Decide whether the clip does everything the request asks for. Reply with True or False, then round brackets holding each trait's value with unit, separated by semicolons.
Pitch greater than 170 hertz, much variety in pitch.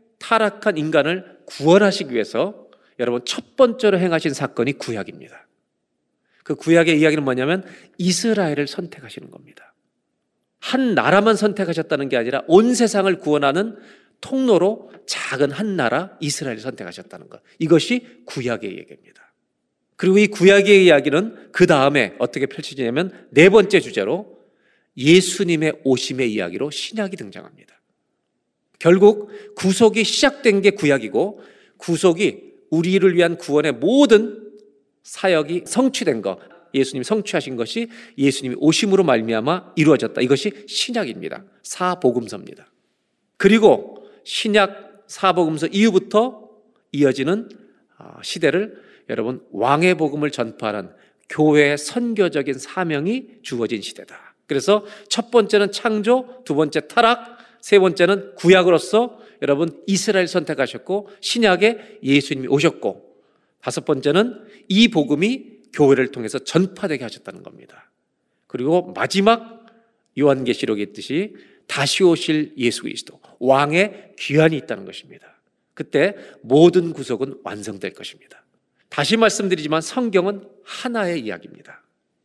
True (185 Hz; 6.3 semitones)